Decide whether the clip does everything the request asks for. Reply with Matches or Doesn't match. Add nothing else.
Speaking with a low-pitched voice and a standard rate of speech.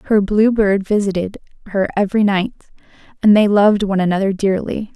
Doesn't match